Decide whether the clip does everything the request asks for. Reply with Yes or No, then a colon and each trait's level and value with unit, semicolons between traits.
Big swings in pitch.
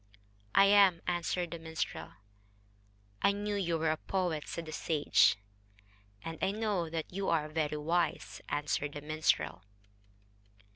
No: average, 3.3 semitones